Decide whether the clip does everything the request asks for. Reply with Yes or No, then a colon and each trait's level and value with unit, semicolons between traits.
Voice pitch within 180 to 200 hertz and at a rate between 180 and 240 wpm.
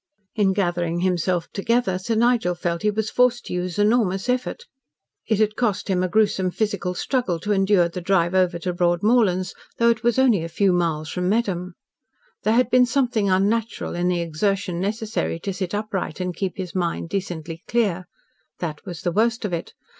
Yes: high, 190 Hz; average, 185 wpm